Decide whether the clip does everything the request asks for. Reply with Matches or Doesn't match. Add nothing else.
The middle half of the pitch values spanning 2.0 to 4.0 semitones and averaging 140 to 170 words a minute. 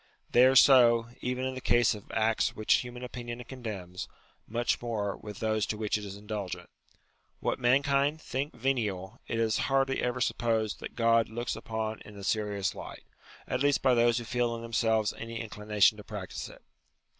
Doesn't match